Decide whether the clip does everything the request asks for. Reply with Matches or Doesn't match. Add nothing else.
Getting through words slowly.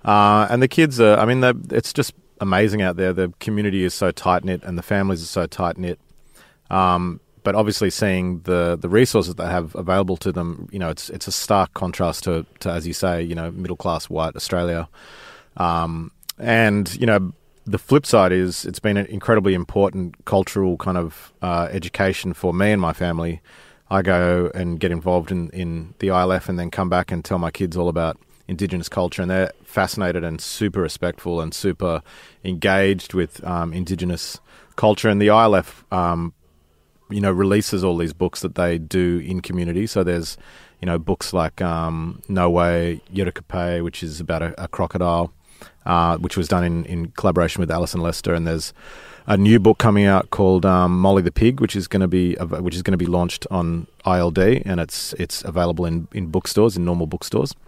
Doesn't match